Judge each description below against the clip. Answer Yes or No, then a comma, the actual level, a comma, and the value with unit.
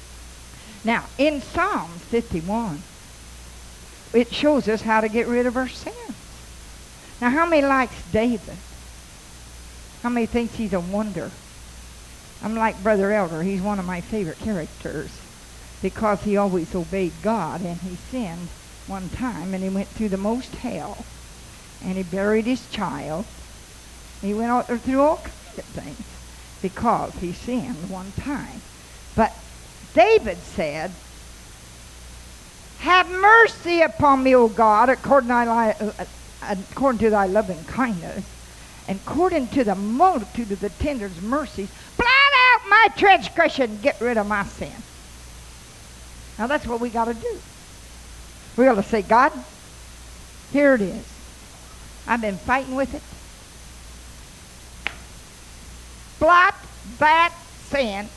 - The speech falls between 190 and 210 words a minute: No, slow, 135 wpm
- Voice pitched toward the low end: No, high, 210 Hz